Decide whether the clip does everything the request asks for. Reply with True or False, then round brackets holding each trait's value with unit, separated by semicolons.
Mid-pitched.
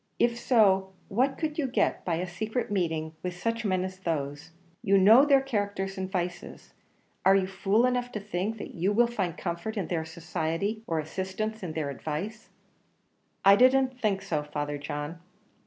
False (195 Hz)